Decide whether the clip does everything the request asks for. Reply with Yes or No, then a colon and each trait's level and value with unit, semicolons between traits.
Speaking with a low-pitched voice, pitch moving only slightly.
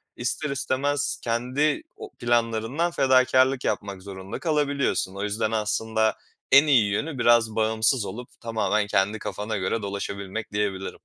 No: low, 115 Hz; average, 4.1 semitones